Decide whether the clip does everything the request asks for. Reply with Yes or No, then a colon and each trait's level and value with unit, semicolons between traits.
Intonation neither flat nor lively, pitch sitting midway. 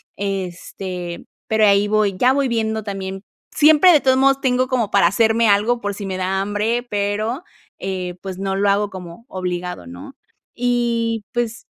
No: average, 3.5 semitones; high, 205 Hz